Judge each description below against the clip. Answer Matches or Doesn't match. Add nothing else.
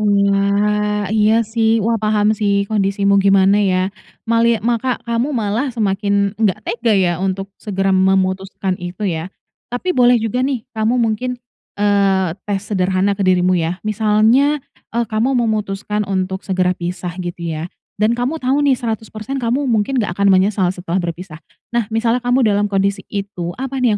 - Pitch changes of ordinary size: Matches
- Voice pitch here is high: Matches